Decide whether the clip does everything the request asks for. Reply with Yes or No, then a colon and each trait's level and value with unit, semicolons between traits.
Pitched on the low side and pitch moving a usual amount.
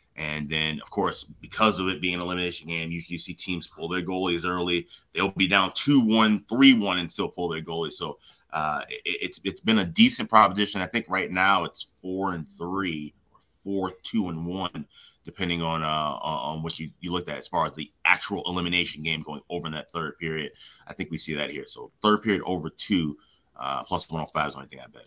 Yes: very low, 90 Hz; average, 3.4 semitones